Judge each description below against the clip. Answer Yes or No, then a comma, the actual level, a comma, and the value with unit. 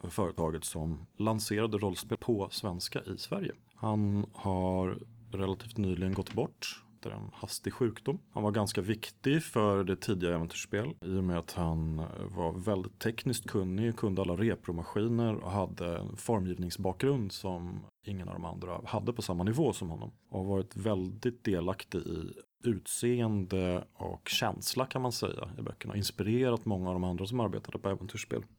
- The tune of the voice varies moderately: Yes, average, 3.5 semitones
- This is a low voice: Yes, low, 105 Hz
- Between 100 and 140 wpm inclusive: No, average, 165 wpm